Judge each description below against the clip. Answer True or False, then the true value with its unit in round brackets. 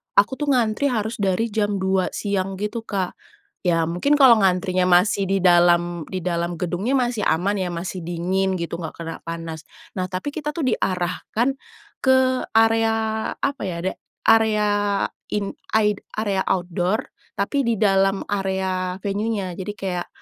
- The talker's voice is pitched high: True (195 Hz)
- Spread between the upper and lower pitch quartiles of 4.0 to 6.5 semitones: False (3.6 semitones)